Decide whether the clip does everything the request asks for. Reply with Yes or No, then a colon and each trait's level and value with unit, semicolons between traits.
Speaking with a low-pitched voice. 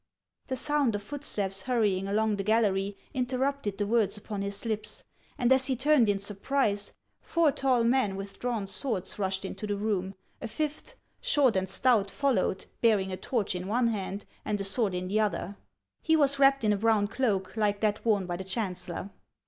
No: high, 210 Hz